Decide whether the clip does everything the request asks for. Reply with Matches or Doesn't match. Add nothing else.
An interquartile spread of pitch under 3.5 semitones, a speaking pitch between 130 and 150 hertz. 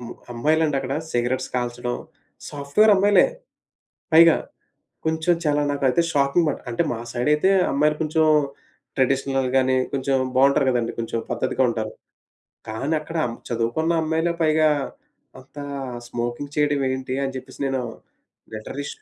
Doesn't match